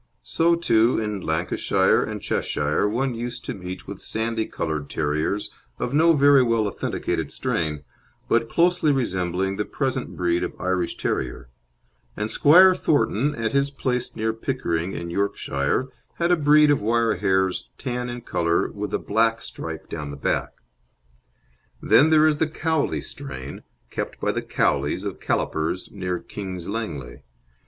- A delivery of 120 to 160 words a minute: Yes, average, 150 wpm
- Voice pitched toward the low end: Yes, low, 110 Hz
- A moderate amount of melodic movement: No, wide, 7.2 semitones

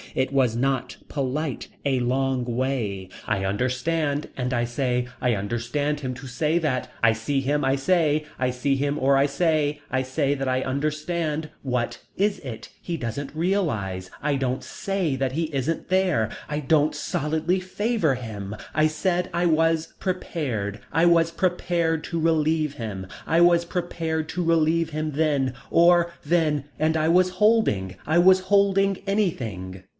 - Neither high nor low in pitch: Yes, medium, 150 Hz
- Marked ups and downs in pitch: No, average, 4.6 semitones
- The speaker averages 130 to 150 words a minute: No, average, 160 wpm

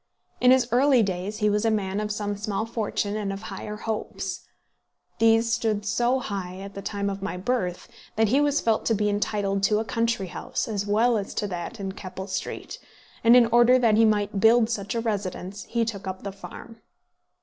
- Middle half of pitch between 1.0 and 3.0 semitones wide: Yes, narrow, 2.6 semitones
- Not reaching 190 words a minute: No, fast, 205 wpm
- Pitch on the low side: No, high, 210 Hz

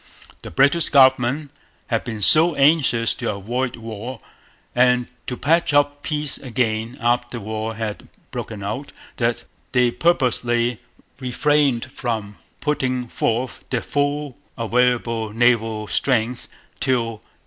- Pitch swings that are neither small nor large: Yes, average, 3.2 semitones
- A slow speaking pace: Yes, slow, 120 wpm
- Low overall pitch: Yes, low, 125 Hz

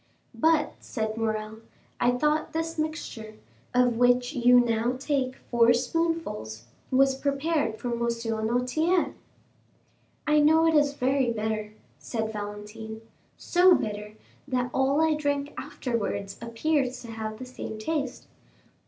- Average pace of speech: No, slow, 125 wpm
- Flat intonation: No, average, 5.0 semitones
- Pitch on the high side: Yes, high, 245 Hz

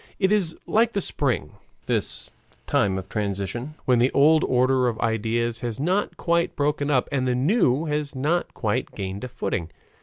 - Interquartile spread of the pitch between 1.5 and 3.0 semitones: No, average, 5.1 semitones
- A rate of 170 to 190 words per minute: Yes, average, 175 wpm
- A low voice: Yes, low, 130 Hz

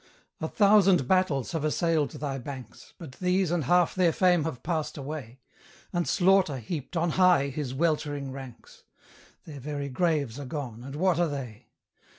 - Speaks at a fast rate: No, average, 165 wpm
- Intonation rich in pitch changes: No, average, 4.4 semitones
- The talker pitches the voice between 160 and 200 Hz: No, medium, 150 Hz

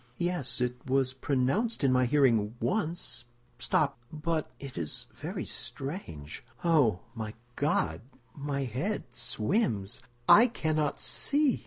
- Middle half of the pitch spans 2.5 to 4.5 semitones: No, average, 5.1 semitones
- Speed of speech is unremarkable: No, slow, 105 wpm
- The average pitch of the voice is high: No, low, 135 Hz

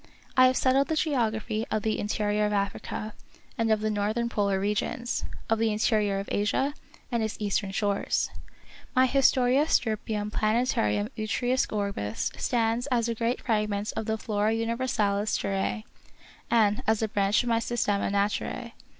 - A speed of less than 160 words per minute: No, average, 165 wpm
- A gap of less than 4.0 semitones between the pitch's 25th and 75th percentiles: Yes, narrow, 2.4 semitones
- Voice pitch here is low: No, high, 220 Hz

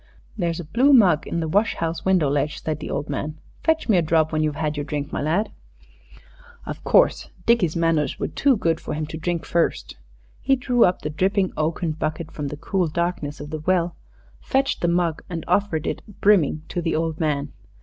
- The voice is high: No, medium, 165 Hz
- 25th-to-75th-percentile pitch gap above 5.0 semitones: No, average, 3.2 semitones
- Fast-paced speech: Yes, fast, 210 wpm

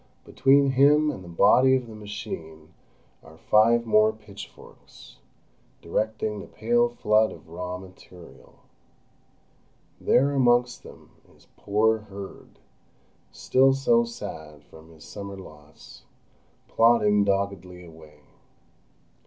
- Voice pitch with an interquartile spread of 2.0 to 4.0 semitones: No, average, 5.1 semitones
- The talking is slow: Yes, slow, 110 wpm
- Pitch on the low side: Yes, low, 105 Hz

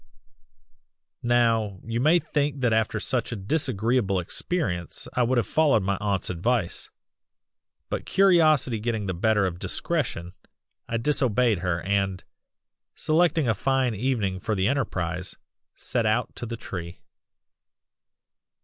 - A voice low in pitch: Yes, low, 115 Hz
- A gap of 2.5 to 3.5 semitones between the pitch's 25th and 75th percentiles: No, average, 5.1 semitones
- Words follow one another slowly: Yes, slow, 130 wpm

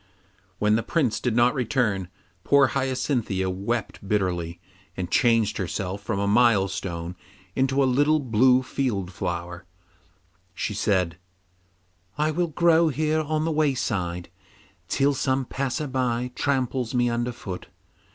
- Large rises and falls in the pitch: Yes, wide, 5.7 semitones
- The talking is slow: Yes, slow, 130 wpm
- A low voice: Yes, low, 120 Hz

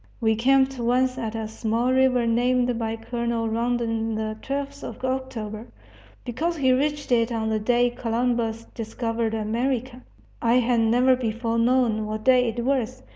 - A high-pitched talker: Yes, high, 235 Hz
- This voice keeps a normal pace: Yes, average, 155 wpm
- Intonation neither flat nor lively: No, narrow, 2.1 semitones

